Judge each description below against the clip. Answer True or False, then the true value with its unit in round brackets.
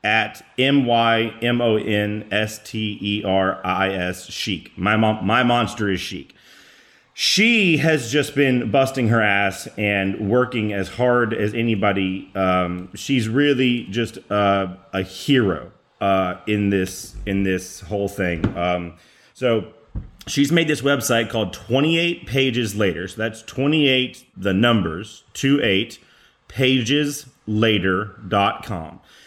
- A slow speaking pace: True (110 wpm)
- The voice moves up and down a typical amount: True (4.6 semitones)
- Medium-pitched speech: False (110 Hz)